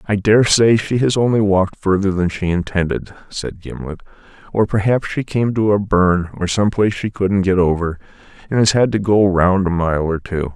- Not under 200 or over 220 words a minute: Yes, fast, 205 wpm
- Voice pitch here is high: No, very low, 95 Hz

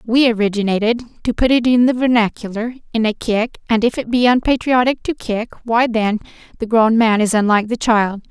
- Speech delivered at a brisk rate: No, average, 195 wpm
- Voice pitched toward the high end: Yes, high, 230 Hz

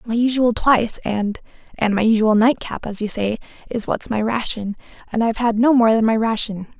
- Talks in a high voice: Yes, high, 225 Hz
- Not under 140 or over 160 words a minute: No, fast, 205 wpm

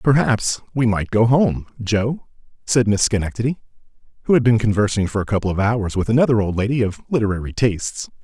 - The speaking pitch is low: Yes, low, 110 Hz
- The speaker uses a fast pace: No, average, 180 wpm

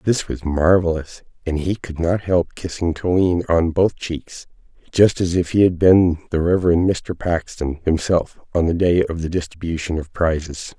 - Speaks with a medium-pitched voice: No, very low, 85 Hz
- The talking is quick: No, average, 180 wpm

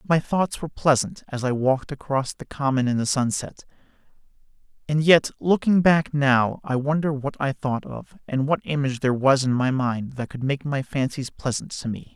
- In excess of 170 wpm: Yes, average, 195 wpm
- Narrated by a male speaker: Yes, male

